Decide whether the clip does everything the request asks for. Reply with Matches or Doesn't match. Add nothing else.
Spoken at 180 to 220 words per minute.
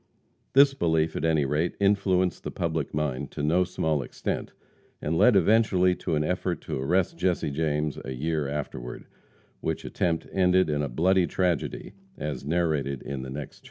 Doesn't match